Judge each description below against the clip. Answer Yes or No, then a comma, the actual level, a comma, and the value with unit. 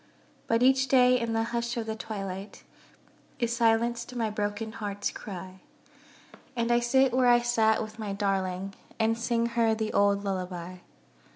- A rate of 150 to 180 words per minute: Yes, average, 160 wpm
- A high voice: Yes, high, 225 Hz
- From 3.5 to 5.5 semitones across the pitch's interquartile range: No, average, 2.8 semitones